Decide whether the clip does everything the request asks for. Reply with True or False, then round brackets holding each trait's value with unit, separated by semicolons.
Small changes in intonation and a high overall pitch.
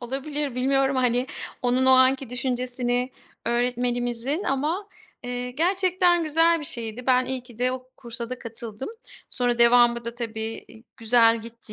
True (2.1 semitones; 250 Hz)